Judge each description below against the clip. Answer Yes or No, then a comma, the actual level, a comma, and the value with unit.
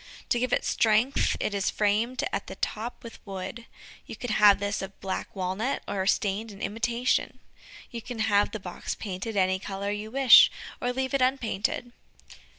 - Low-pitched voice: No, high, 215 Hz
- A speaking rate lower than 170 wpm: No, average, 175 wpm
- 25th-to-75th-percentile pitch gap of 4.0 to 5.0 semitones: No, average, 3.4 semitones